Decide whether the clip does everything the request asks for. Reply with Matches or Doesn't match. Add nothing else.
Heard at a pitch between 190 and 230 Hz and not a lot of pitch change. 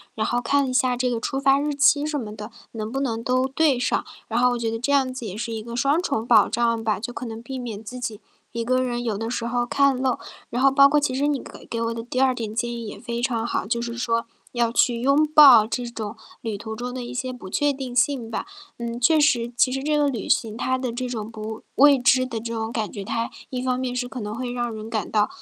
Doesn't match